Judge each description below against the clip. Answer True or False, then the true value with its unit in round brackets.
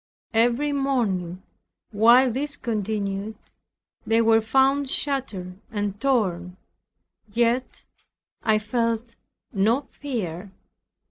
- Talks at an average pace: False (85 wpm)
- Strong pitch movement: False (4.2 semitones)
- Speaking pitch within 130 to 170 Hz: False (225 Hz)